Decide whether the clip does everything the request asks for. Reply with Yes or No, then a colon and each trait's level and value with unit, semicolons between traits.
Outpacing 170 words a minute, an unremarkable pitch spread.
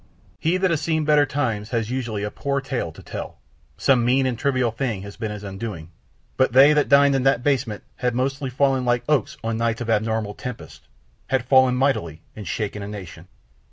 Yes: average, 200 wpm; average, 3.9 semitones